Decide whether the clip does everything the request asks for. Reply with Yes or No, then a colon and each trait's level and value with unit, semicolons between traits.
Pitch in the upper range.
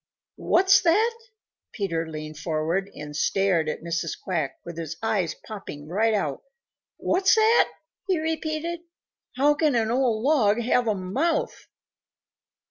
Yes: high, 215 Hz